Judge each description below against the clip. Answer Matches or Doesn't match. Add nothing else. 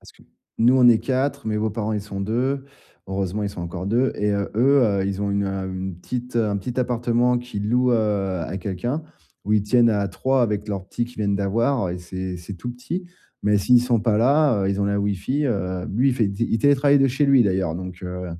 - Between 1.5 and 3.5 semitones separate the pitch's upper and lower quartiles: Doesn't match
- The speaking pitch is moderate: Doesn't match